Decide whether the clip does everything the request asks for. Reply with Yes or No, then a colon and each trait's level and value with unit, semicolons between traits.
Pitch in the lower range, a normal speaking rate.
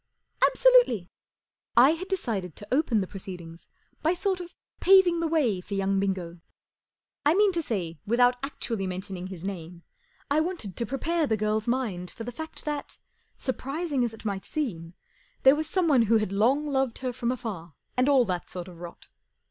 No: high, 235 Hz; average, 190 wpm